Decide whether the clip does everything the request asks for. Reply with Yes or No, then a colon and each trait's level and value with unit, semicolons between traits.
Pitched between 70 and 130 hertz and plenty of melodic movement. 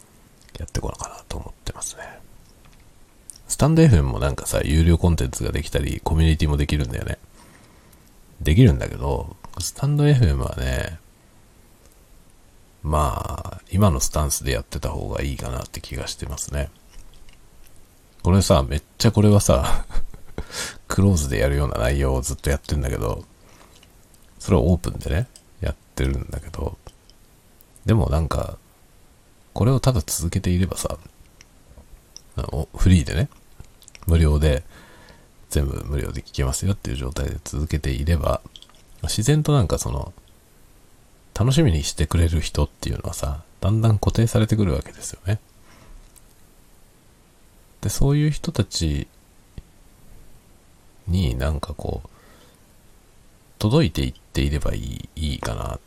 Yes: very low, 90 Hz; wide, 5.8 semitones